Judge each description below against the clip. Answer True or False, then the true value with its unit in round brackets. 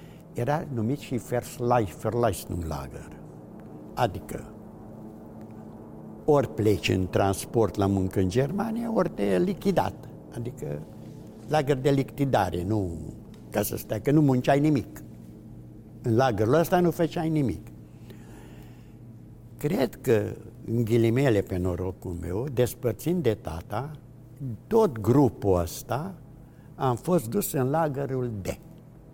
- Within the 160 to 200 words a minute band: False (115 wpm)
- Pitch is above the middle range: False (120 Hz)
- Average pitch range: False (5.8 semitones)